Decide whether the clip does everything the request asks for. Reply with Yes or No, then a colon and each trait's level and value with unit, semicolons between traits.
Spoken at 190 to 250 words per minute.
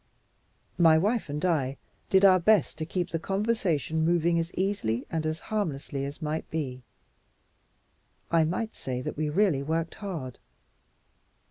No: average, 145 wpm